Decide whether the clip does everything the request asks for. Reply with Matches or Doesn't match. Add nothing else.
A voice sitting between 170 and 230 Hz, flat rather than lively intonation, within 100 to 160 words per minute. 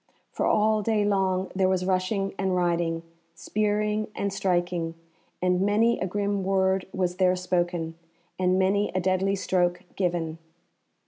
Matches